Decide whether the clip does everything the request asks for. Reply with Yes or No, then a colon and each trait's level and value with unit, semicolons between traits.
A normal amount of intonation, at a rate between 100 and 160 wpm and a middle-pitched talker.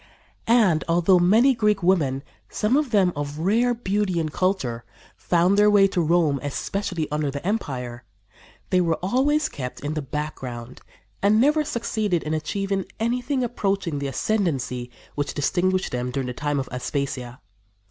No: wide, 6.6 semitones; average, 155 wpm; medium, 175 Hz